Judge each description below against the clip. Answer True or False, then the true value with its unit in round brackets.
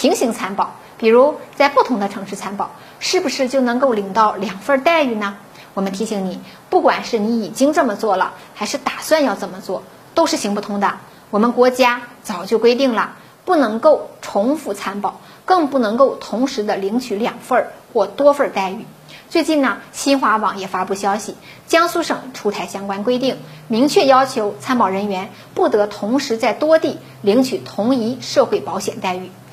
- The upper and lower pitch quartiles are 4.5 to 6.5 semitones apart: True (5.4 semitones)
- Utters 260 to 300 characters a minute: True (270 characters per minute)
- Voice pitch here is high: True (230 Hz)